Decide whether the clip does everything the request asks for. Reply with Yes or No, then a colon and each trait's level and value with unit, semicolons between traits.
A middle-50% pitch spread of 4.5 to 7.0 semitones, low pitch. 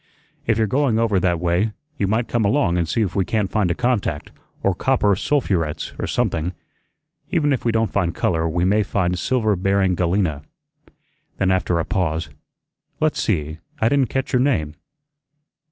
Yes: average, 4.8 semitones; low, 100 Hz